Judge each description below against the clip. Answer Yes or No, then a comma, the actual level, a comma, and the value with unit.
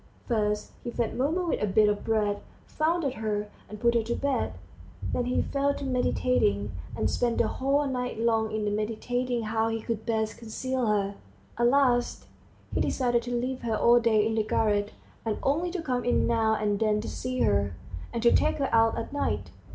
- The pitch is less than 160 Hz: No, high, 230 Hz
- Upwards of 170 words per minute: Yes, average, 200 wpm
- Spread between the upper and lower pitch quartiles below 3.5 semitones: Yes, average, 2.9 semitones